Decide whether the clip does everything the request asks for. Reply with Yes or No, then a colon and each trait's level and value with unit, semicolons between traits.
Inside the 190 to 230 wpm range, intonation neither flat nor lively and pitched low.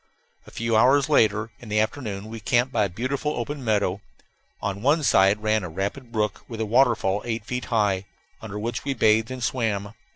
Yes: average, 195 wpm; average, 3.4 semitones; low, 110 Hz